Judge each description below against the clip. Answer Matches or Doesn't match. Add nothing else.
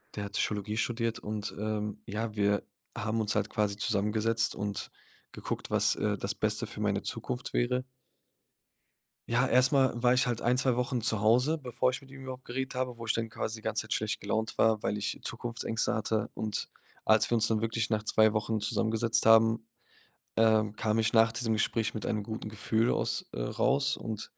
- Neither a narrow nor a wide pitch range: Doesn't match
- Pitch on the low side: Matches